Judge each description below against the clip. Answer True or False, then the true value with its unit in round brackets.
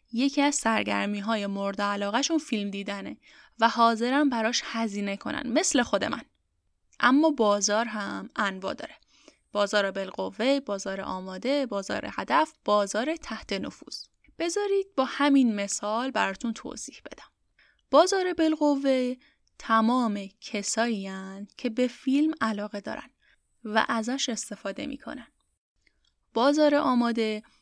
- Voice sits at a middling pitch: False (230 Hz)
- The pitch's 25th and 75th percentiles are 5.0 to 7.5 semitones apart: True (5.4 semitones)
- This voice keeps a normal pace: True (115 wpm)